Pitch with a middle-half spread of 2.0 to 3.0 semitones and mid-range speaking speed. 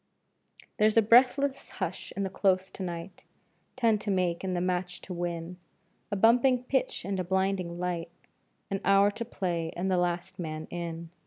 Yes: average, 2.7 semitones; average, 175 wpm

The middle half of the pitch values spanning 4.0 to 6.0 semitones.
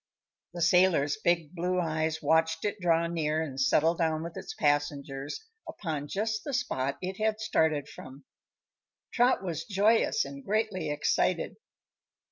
Yes: average, 4.9 semitones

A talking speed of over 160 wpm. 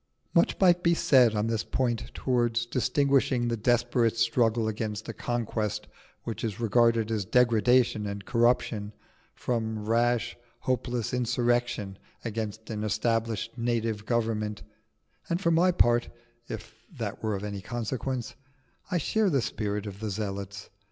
No: average, 140 wpm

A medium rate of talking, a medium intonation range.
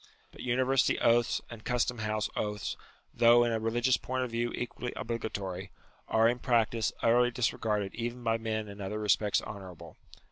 No: average, 170 wpm; narrow, 2.0 semitones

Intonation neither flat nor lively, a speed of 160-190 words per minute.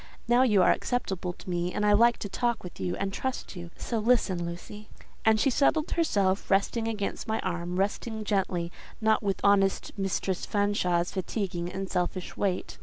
Yes: average, 3.4 semitones; average, 170 wpm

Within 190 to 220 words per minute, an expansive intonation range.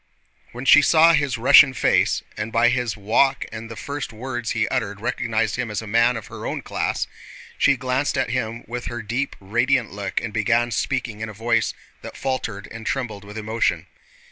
No: average, 195 wpm; average, 2.8 semitones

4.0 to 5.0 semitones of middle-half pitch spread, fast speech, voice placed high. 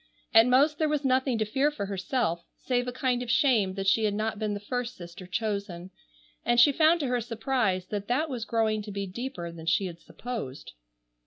Yes: average, 4.5 semitones; fast, 215 wpm; high, 225 Hz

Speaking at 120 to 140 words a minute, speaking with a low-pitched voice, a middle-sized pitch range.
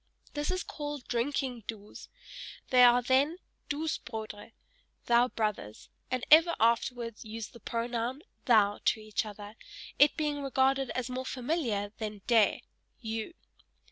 No: slow, 135 wpm; high, 240 Hz; average, 3.7 semitones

